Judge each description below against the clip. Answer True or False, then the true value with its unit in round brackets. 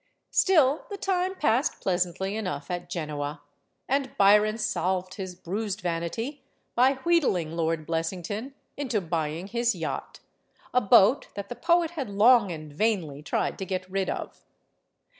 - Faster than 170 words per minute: False (140 wpm)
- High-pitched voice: True (195 Hz)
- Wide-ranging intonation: True (6.4 semitones)